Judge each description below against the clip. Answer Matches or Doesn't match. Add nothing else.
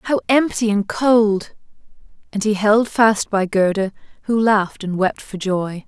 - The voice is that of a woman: Matches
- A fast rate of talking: Doesn't match